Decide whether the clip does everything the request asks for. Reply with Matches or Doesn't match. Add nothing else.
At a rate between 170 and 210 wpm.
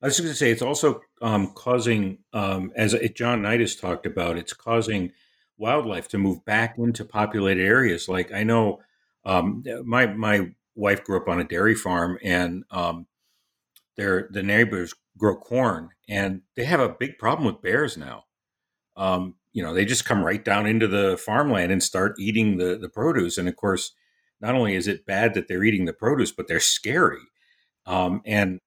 Matches